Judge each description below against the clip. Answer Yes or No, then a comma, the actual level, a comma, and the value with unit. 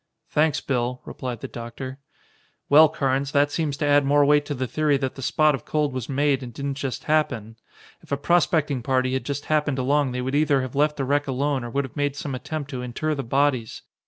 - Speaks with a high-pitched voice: No, medium, 140 Hz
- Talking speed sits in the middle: No, fast, 225 wpm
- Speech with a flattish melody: Yes, narrow, 2.1 semitones